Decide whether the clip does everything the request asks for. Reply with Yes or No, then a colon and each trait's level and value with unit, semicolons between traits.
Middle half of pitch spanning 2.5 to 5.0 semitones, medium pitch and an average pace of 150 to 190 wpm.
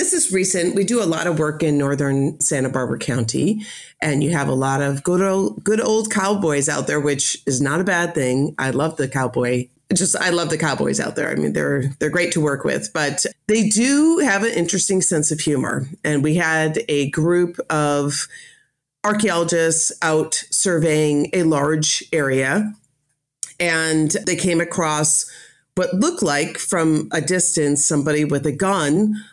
Yes: average, 4.4 semitones; medium, 160 Hz; average, 180 wpm